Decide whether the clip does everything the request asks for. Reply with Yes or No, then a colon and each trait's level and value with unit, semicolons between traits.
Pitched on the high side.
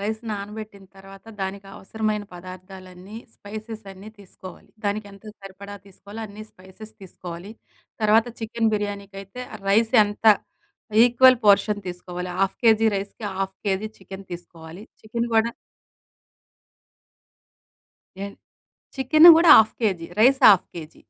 Yes: high, 200 Hz